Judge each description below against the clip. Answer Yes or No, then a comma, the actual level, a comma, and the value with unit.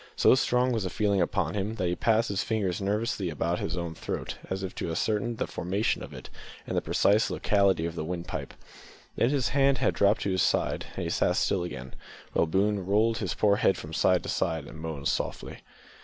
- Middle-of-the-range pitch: No, low, 100 Hz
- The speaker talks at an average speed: No, fast, 215 wpm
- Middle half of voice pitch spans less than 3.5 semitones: No, average, 4.1 semitones